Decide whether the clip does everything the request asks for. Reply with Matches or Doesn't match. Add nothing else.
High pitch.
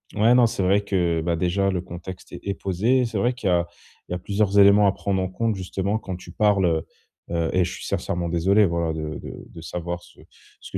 Doesn't match